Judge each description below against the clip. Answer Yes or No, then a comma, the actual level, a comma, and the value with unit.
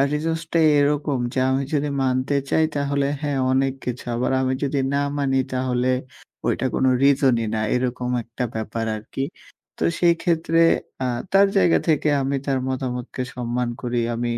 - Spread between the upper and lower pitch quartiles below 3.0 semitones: Yes, narrow, 2.6 semitones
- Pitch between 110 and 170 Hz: Yes, low, 135 Hz